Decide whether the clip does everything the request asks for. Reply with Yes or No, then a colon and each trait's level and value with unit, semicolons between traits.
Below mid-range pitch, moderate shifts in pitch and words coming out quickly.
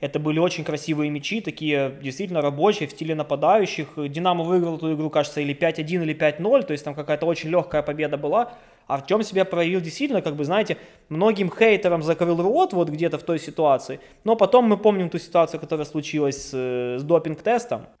No: medium, 160 Hz; average, 3.5 semitones; fast, 190 wpm